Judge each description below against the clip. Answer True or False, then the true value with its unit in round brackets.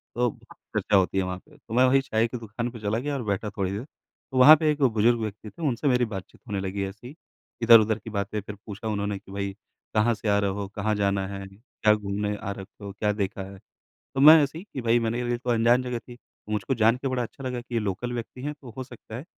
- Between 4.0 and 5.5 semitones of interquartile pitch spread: False (3.4 semitones)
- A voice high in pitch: False (110 Hz)